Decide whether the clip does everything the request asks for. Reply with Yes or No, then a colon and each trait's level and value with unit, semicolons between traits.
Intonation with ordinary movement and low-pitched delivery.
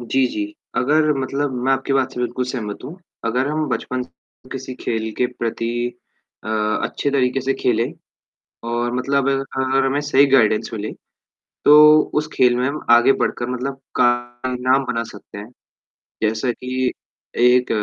No: narrow, 2.1 semitones; low, 125 Hz